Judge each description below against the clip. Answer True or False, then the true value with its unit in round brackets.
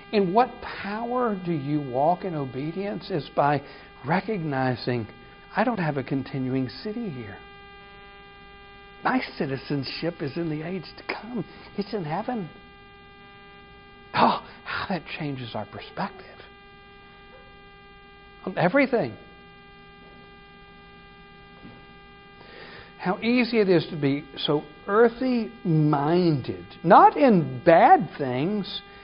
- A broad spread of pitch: True (7.0 semitones)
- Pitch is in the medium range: True (180 Hz)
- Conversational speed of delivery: False (100 wpm)